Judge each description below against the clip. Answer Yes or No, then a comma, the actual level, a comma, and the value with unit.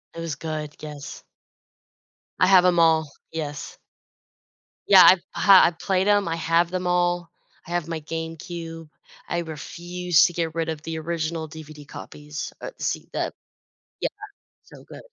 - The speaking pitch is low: No, medium, 165 Hz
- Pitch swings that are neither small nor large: No, narrow, 1.9 semitones